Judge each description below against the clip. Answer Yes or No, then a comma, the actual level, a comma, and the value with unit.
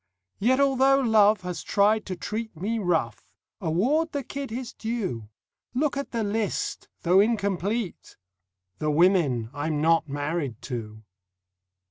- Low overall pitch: No, high, 200 Hz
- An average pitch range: No, wide, 6.6 semitones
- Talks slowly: Yes, slow, 130 wpm